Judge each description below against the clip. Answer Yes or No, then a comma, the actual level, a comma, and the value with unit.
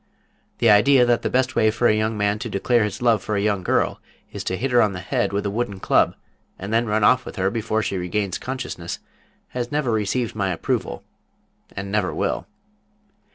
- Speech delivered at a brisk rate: Yes, fast, 210 wpm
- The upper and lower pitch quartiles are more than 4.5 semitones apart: No, average, 3.2 semitones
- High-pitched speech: No, low, 110 Hz